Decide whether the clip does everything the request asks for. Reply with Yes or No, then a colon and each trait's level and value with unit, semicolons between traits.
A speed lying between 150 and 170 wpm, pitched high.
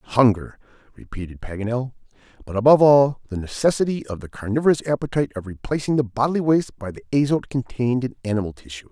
No: average, 160 wpm; low, 125 Hz